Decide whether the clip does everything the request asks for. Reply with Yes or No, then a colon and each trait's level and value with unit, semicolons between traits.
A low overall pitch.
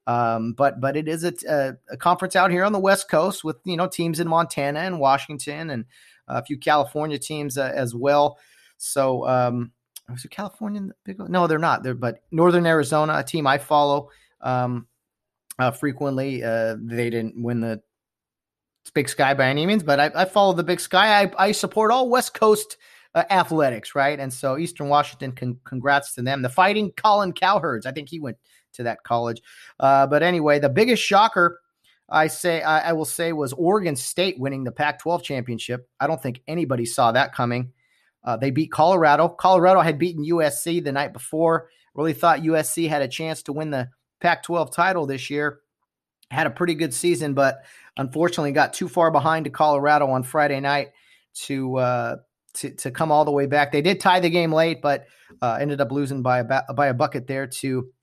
No: medium, 150 Hz